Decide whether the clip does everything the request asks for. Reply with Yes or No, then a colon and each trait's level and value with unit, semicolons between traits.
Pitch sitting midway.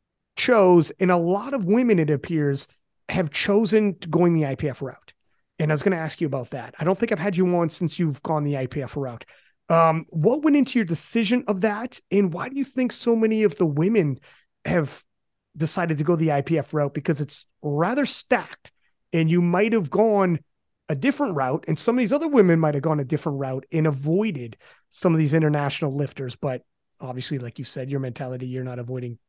Yes: medium, 160 Hz